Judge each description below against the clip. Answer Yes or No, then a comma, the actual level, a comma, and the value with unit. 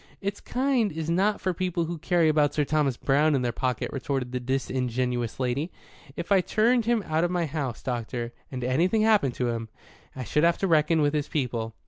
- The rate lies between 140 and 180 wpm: No, fast, 205 wpm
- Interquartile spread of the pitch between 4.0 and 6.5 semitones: Yes, wide, 5.6 semitones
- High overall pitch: No, medium, 150 Hz